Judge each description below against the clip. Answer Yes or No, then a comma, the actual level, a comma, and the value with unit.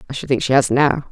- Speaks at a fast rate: Yes, fast, 320 wpm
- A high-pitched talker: No, low, 135 Hz